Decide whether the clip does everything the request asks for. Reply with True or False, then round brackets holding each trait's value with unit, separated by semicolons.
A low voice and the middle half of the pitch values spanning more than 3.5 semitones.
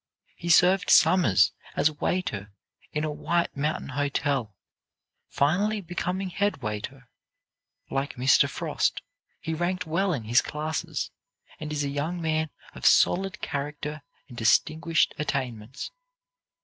False (150 Hz; 4.3 semitones)